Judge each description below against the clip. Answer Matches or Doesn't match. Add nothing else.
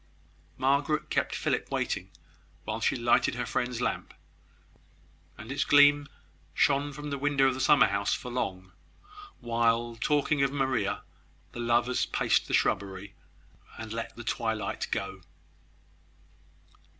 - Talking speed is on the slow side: Matches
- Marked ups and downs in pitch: Doesn't match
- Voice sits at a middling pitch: Doesn't match